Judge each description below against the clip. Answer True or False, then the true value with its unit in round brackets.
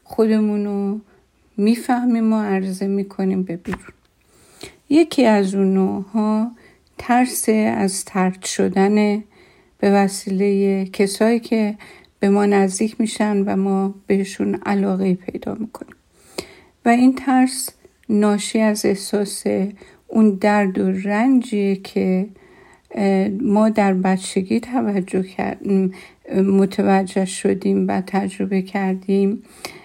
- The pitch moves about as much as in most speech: False (2.1 semitones)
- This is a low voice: False (200 Hz)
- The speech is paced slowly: True (100 wpm)